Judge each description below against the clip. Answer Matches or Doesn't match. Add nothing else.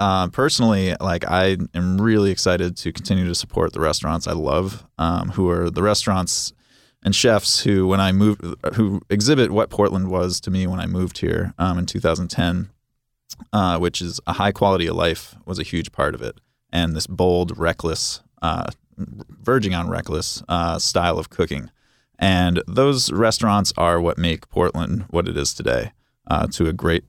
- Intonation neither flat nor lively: Matches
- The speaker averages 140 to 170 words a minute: Doesn't match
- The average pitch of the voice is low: Matches